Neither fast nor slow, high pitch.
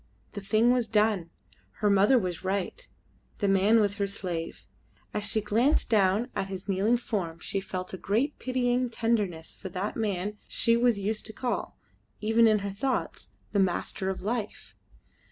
Yes: average, 170 wpm; high, 210 Hz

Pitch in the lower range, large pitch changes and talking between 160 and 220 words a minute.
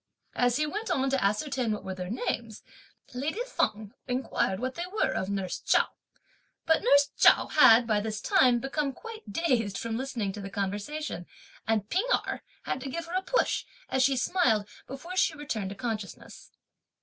No: very high, 250 Hz; wide, 6.1 semitones; average, 180 wpm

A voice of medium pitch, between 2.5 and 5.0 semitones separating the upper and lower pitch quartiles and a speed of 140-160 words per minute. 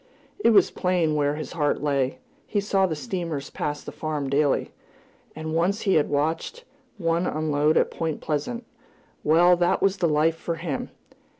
No: medium, 160 Hz; average, 3.2 semitones; average, 170 wpm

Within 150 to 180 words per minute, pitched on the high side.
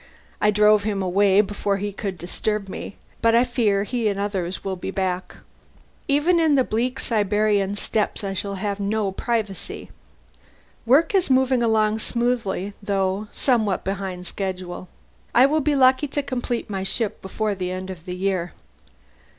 Yes: average, 160 wpm; high, 205 Hz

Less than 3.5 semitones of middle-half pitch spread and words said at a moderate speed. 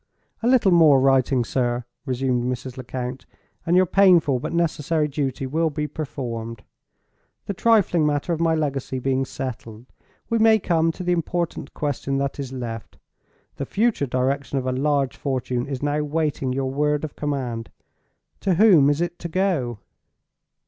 No: average, 4.2 semitones; average, 160 wpm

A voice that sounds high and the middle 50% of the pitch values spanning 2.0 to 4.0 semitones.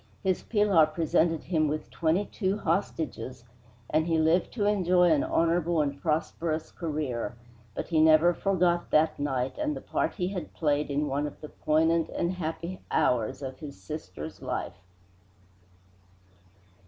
No: medium, 160 Hz; average, 3.0 semitones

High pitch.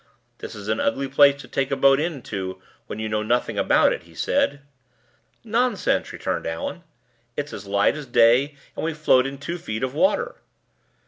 No: low, 135 Hz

